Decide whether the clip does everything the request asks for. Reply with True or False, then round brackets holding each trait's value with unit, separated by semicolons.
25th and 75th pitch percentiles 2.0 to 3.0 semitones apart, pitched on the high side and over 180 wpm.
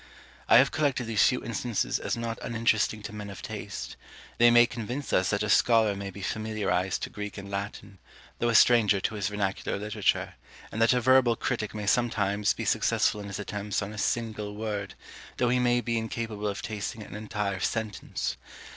False (2.4 semitones; 105 Hz; 190 wpm)